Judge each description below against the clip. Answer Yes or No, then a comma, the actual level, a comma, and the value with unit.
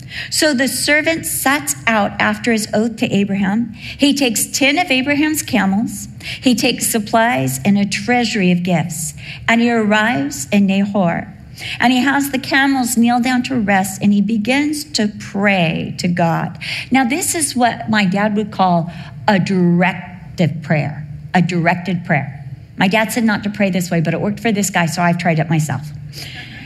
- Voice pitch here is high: Yes, high, 200 Hz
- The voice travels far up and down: Yes, wide, 5.7 semitones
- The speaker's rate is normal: Yes, average, 175 wpm